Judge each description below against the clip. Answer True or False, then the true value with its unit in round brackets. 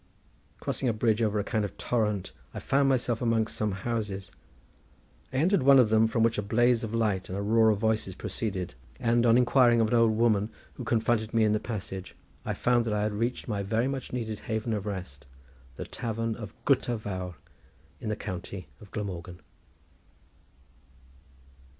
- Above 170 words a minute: True (180 wpm)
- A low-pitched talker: True (110 Hz)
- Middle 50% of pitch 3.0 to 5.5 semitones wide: False (2.4 semitones)